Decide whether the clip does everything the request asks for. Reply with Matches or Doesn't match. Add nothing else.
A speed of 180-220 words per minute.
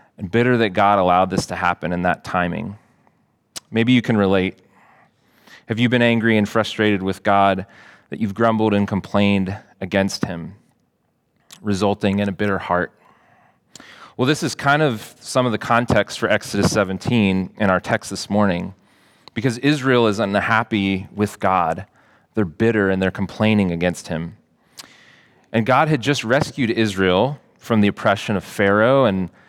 Doesn't match